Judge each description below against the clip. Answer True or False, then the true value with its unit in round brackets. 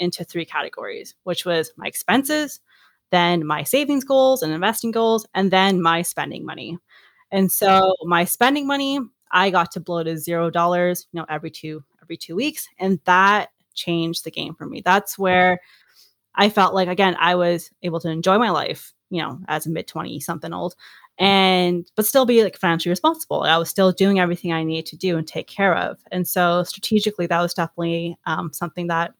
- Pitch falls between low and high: True (180 Hz)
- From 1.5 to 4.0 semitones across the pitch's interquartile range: True (2.7 semitones)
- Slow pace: False (195 wpm)